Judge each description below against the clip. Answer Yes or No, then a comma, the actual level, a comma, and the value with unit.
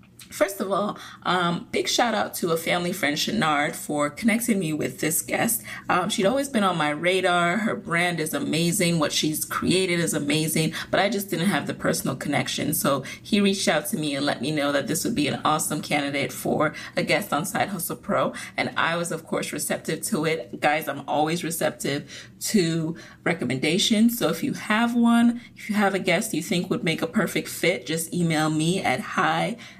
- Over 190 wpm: Yes, fast, 205 wpm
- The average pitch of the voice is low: No, medium, 170 Hz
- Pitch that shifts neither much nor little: Yes, average, 4.4 semitones